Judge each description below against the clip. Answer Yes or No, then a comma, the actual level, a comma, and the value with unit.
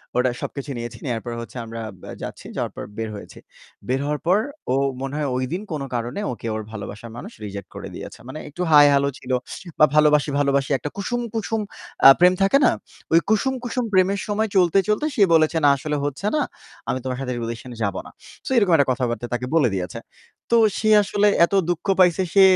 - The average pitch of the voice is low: No, medium, 145 Hz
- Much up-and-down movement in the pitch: Yes, wide, 7.2 semitones